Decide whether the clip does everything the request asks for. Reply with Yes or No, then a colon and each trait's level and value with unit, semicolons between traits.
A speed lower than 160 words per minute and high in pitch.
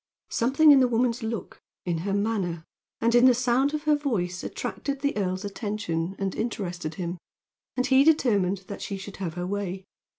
No: average, 185 wpm; high, 205 Hz